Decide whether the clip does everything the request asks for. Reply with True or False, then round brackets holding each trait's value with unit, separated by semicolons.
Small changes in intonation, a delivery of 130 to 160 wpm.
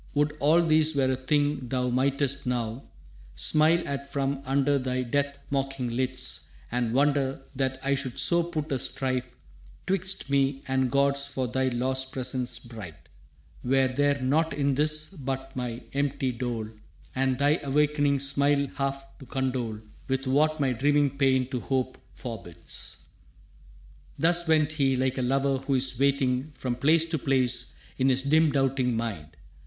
True (1.9 semitones; 155 wpm)